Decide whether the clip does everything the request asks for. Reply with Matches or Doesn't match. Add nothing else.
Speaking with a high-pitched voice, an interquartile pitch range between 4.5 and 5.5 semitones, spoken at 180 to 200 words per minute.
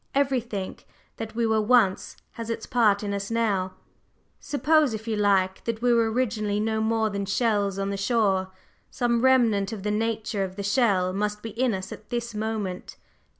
Doesn't match